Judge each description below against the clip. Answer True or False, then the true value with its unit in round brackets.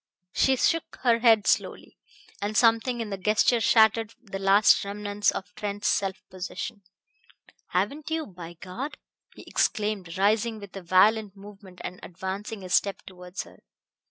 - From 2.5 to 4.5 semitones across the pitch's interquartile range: True (2.8 semitones)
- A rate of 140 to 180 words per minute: True (150 wpm)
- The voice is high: True (205 Hz)